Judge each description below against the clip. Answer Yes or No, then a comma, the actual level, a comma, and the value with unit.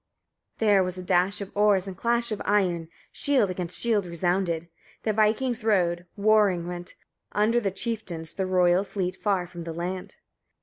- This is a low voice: No, high, 190 Hz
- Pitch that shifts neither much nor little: Yes, average, 3.1 semitones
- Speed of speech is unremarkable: Yes, average, 170 wpm